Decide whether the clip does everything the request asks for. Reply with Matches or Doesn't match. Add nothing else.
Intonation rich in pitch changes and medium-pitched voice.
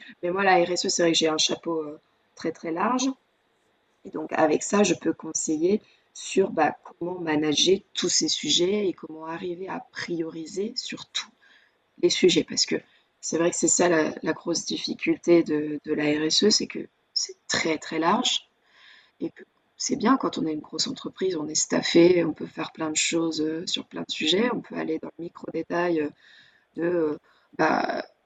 Doesn't match